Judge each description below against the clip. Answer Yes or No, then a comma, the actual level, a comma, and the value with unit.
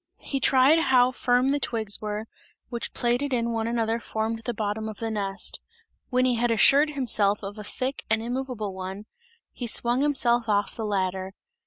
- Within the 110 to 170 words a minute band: No, average, 185 wpm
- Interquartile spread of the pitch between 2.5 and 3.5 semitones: Yes, average, 3.2 semitones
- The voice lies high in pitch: Yes, high, 230 Hz